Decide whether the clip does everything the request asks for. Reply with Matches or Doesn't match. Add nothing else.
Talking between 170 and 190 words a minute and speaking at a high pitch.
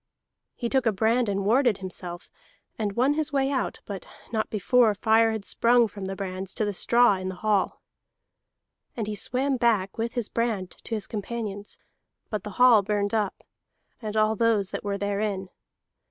Matches